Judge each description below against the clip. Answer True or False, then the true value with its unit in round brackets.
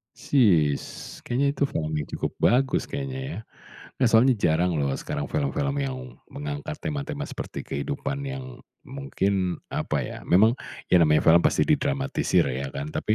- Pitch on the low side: True (130 Hz)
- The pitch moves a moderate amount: False (8.5 semitones)